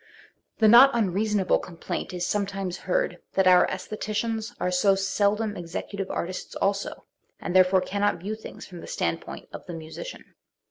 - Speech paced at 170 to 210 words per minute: No, average, 150 wpm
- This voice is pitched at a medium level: No, high, 195 Hz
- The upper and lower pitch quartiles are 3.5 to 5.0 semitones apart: No, average, 2.7 semitones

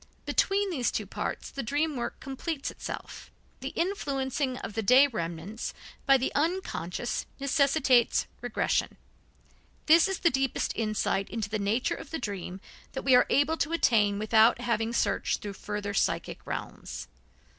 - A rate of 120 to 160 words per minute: Yes, average, 150 wpm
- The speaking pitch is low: No, very high, 250 Hz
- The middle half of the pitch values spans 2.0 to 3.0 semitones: No, average, 5.0 semitones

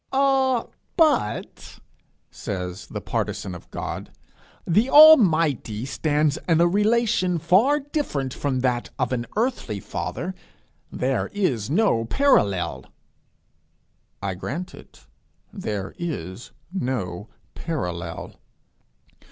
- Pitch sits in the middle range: Yes, medium, 150 Hz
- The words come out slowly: Yes, slow, 100 wpm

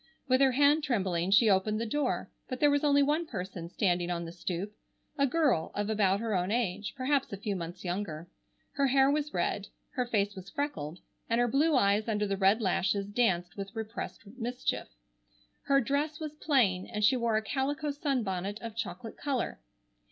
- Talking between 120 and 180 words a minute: No, average, 190 wpm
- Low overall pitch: No, high, 220 Hz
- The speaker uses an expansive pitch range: Yes, wide, 6.2 semitones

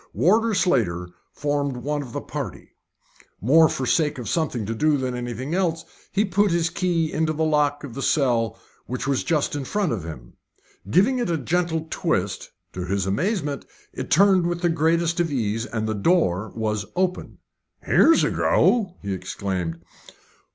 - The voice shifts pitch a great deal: Yes, wide, 7.0 semitones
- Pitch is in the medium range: Yes, medium, 150 Hz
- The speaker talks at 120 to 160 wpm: No, average, 170 wpm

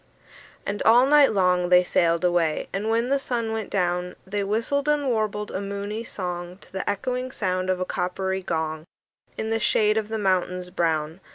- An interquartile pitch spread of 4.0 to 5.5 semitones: No, average, 3.6 semitones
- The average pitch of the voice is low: No, high, 195 Hz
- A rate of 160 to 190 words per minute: Yes, average, 185 wpm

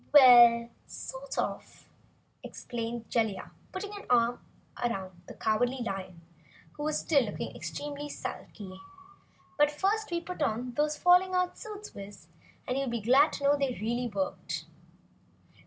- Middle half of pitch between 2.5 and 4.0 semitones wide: No, average, 5.0 semitones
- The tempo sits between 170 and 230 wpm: No, average, 140 wpm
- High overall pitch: Yes, very high, 250 Hz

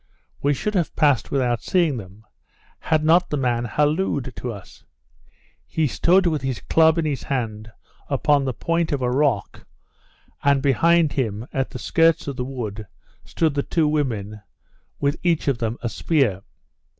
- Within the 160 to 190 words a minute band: Yes, average, 165 wpm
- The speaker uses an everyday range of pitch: Yes, average, 4.8 semitones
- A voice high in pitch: No, medium, 140 Hz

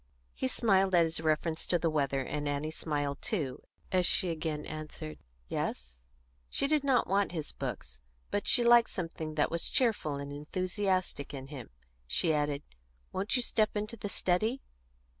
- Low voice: No, medium, 160 Hz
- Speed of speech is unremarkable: Yes, average, 165 wpm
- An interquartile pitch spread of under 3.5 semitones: No, average, 5.2 semitones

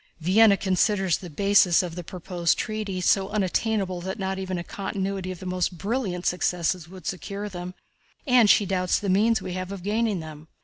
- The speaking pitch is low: No, high, 190 Hz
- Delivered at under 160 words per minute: No, average, 180 wpm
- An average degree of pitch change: No, narrow, 2.1 semitones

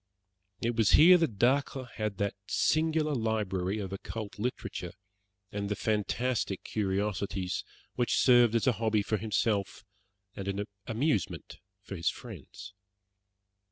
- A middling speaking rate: No, slow, 125 wpm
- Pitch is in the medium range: No, low, 110 Hz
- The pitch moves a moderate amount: Yes, average, 3.5 semitones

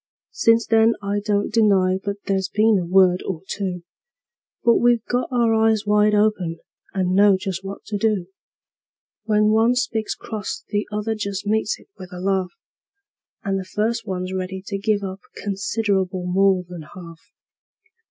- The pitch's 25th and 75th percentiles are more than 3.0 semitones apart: No, narrow, 2.5 semitones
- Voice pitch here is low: No, high, 200 Hz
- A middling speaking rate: Yes, average, 160 wpm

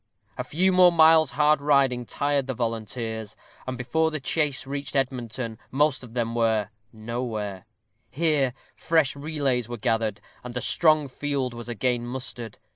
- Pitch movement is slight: No, average, 3.8 semitones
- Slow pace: No, average, 150 wpm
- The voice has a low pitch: Yes, low, 130 Hz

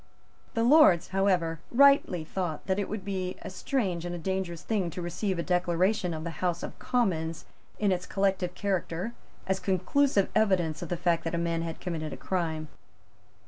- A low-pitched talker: No, medium, 180 Hz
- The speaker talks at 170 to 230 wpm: Yes, average, 185 wpm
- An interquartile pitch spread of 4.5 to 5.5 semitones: No, average, 2.7 semitones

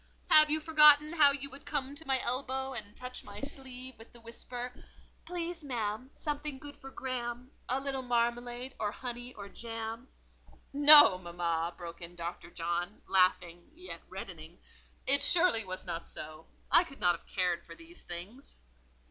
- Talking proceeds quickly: No, average, 160 wpm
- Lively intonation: Yes, wide, 6.0 semitones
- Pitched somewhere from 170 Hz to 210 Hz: No, very high, 250 Hz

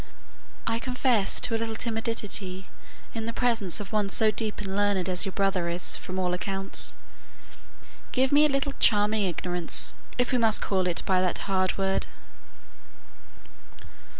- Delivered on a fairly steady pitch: No, average, 3.4 semitones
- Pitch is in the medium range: No, high, 205 Hz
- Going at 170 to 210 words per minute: No, average, 155 wpm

